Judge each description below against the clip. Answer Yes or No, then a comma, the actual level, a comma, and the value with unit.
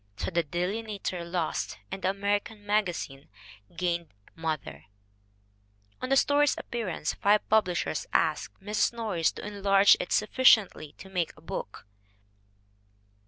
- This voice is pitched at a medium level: No, high, 195 Hz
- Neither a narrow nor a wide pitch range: Yes, average, 3.7 semitones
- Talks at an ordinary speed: No, slow, 120 wpm